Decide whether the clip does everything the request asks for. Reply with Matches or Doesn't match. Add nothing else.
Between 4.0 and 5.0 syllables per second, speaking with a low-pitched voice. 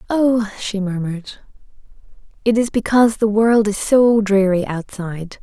Doesn't match